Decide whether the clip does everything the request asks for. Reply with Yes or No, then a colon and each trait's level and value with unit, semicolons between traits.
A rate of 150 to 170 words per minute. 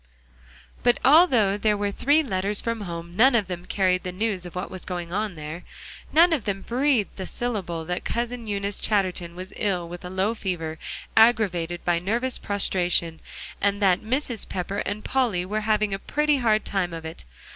No: average, 185 wpm